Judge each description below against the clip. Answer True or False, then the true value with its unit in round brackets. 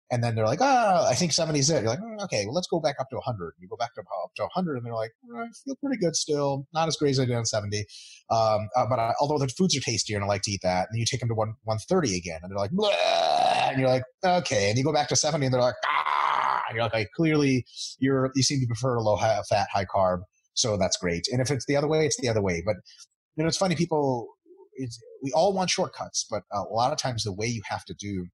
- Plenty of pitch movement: True (6.8 semitones)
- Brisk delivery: True (290 wpm)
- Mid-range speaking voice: False (130 Hz)